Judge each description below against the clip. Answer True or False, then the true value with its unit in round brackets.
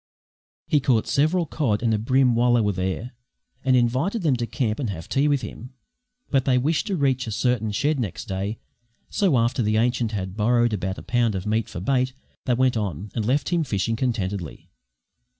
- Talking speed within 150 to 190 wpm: False (205 wpm)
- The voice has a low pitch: True (120 Hz)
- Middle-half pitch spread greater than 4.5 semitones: False (3.8 semitones)